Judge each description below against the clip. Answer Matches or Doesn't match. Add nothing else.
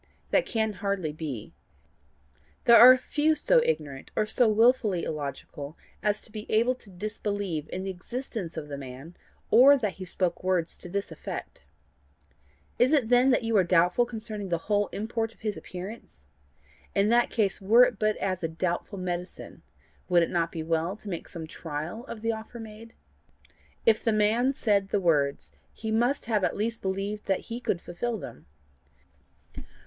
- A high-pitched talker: Matches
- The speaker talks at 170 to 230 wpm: Matches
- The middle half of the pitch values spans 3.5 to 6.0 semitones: Matches